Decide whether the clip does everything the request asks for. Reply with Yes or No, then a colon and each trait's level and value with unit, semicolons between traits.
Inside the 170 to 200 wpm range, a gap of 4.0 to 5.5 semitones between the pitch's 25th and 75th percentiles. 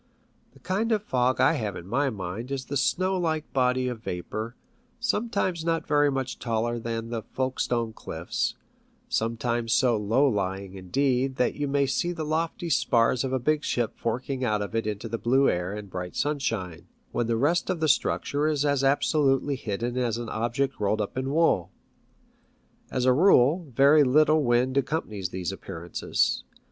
Yes: average, 175 wpm; average, 4.5 semitones